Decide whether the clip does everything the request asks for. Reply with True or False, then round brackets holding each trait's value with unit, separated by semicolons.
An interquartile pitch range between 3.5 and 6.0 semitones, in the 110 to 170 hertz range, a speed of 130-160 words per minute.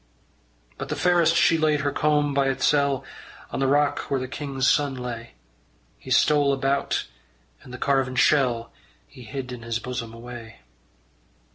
False (2.6 semitones; 135 Hz; 155 wpm)